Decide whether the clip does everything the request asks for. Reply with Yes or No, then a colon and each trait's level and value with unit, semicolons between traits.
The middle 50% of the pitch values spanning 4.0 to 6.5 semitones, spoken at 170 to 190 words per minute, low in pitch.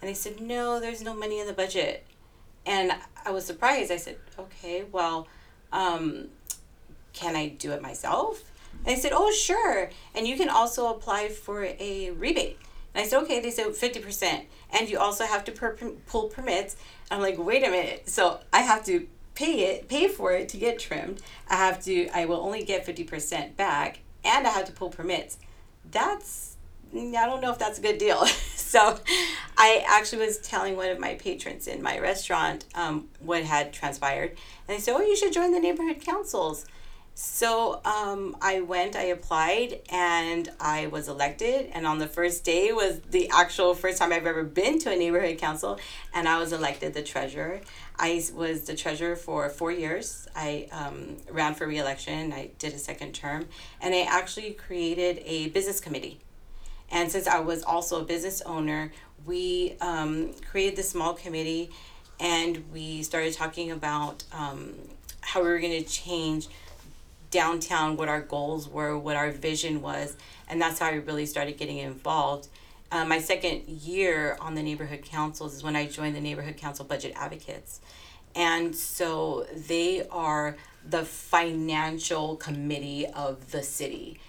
No: average, 4.7 semitones; average, 175 wpm; medium, 170 Hz